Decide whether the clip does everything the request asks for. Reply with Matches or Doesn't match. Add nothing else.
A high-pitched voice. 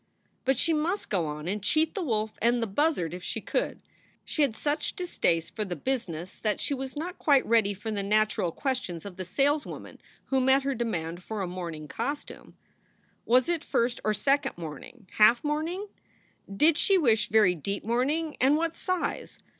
Matches